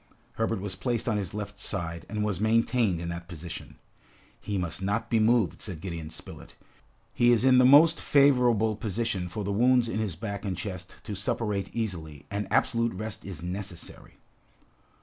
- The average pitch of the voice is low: Yes, low, 105 Hz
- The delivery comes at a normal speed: Yes, average, 175 wpm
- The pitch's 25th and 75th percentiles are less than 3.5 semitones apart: No, average, 4.1 semitones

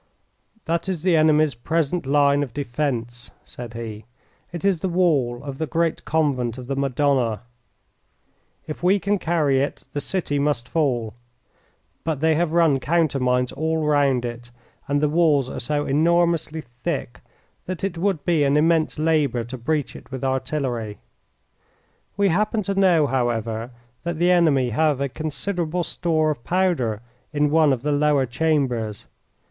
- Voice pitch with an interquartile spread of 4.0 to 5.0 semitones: Yes, average, 4.4 semitones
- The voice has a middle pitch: Yes, medium, 150 Hz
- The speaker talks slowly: No, average, 155 wpm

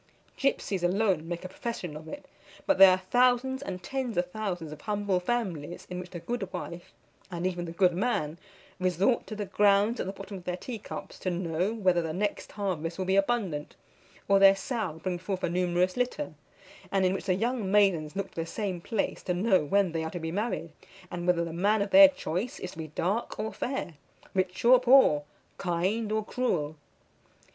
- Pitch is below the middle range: No, high, 190 Hz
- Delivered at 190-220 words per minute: Yes, fast, 205 wpm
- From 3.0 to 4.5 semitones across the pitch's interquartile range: Yes, average, 3.6 semitones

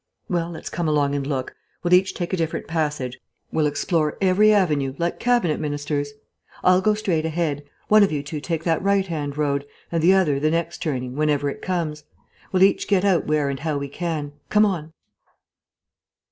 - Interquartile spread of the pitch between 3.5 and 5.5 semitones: Yes, average, 3.9 semitones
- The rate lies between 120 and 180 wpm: No, average, 190 wpm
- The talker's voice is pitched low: No, medium, 160 Hz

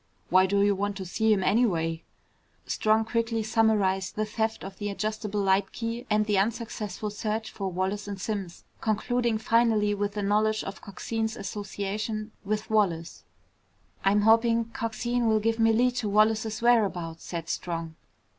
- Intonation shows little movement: Yes, narrow, 2.2 semitones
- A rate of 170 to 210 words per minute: No, average, 160 wpm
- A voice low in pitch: No, high, 215 Hz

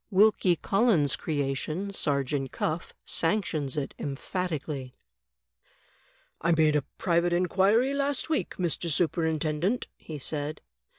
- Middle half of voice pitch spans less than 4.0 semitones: No, average, 4.5 semitones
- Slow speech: Yes, slow, 105 wpm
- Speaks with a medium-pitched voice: Yes, medium, 165 Hz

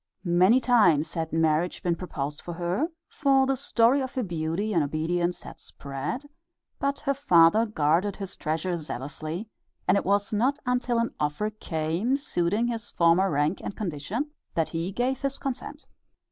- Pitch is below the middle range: No, medium, 185 Hz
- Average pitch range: No, wide, 6.8 semitones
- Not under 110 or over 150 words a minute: No, average, 160 wpm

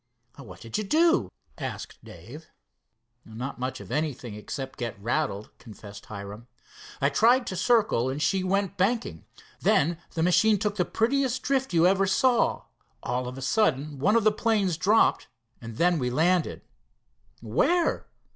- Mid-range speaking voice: Yes, medium, 170 Hz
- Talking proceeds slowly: No, average, 155 wpm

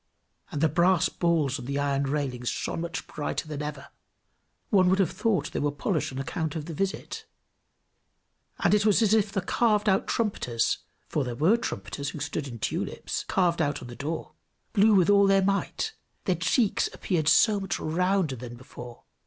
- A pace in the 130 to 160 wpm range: No, average, 185 wpm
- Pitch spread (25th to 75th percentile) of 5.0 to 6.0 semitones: Yes, wide, 5.5 semitones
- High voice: No, medium, 165 Hz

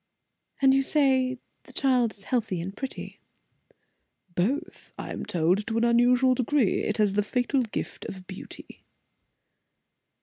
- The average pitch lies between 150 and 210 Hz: No, high, 240 Hz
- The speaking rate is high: No, average, 140 wpm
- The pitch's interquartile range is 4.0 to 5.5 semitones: Yes, average, 4.4 semitones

